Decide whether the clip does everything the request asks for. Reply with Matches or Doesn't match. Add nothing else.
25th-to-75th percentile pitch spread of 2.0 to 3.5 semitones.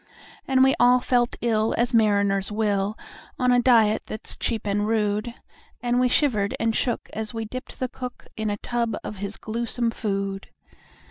Matches